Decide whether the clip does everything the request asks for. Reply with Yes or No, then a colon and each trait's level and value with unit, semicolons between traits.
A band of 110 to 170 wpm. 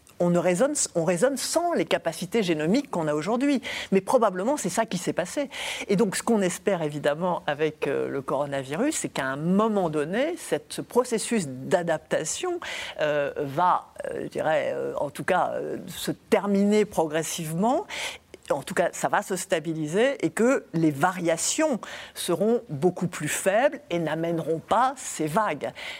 Yes: average, 160 wpm